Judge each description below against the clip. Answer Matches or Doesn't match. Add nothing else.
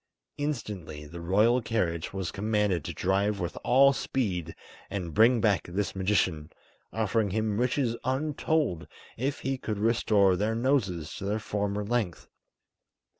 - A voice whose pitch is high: Doesn't match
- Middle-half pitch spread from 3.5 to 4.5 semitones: Matches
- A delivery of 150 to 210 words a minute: Doesn't match